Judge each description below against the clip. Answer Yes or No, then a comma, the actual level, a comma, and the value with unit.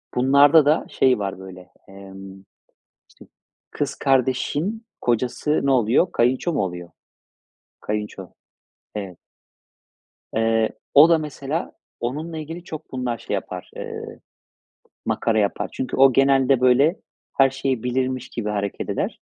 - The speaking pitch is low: Yes, low, 130 Hz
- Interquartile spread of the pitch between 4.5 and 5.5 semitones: Yes, average, 5.1 semitones